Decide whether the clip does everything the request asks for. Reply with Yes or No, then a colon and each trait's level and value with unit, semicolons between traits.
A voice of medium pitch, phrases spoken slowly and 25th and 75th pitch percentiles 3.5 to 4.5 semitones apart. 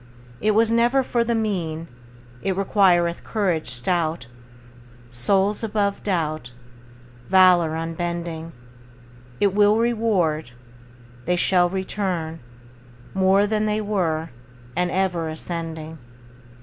Yes: medium, 180 Hz; slow, 100 wpm; average, 4.0 semitones